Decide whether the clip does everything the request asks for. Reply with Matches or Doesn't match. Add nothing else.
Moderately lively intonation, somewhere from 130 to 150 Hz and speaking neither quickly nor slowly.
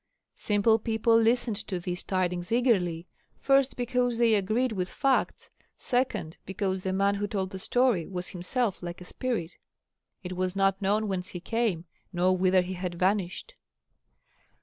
Doesn't match